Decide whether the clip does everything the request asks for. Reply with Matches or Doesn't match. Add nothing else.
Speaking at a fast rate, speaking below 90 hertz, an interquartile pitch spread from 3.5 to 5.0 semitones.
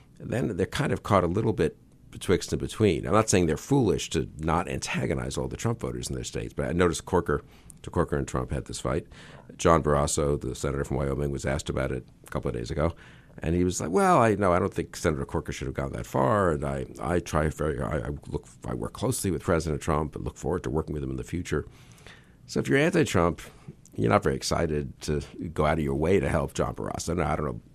Matches